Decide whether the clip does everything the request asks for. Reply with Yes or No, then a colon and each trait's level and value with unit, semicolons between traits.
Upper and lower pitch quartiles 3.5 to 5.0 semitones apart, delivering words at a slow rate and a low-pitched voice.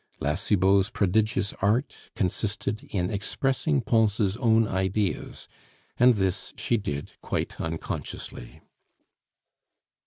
No: average, 3.0 semitones; slow, 95 wpm; low, 105 Hz